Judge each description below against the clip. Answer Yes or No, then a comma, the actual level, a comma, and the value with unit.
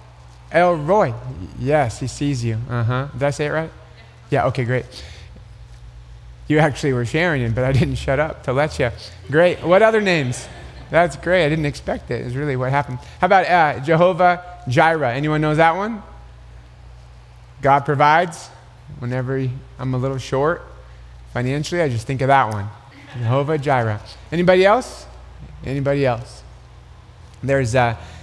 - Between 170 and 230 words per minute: No, average, 160 wpm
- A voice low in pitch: Yes, low, 130 Hz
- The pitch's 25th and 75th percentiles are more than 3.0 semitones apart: Yes, average, 4.8 semitones